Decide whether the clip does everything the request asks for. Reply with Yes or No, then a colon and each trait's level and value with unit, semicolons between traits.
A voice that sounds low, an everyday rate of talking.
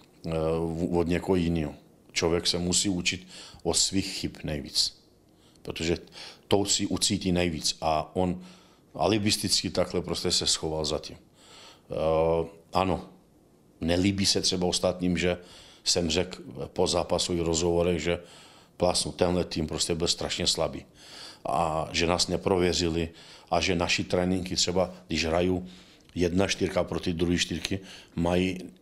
Yes: very low, 90 Hz; average, 130 wpm